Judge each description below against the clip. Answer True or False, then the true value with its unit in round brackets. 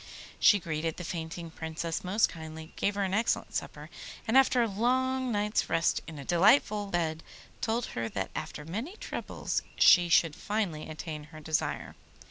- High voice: False (175 Hz)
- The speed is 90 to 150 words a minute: False (165 wpm)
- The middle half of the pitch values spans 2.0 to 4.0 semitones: False (5.2 semitones)